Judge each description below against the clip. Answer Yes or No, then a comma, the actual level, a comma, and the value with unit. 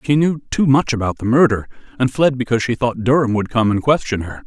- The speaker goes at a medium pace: No, fast, 240 wpm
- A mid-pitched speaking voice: No, low, 125 Hz